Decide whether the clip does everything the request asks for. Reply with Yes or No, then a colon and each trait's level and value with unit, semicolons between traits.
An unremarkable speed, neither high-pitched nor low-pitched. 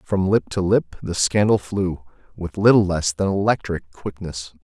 No: average, 170 wpm; very low, 95 Hz